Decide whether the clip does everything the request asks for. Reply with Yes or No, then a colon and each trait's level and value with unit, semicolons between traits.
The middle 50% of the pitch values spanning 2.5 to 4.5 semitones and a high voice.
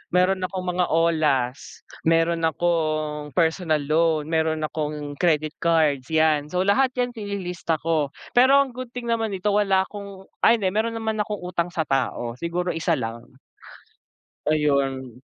No: average, 4.1 semitones; medium, 165 Hz